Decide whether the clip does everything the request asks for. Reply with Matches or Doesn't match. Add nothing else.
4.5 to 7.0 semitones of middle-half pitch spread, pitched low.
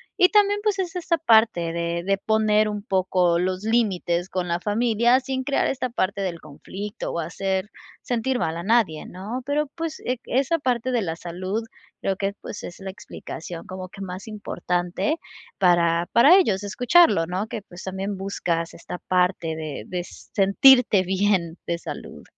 Doesn't match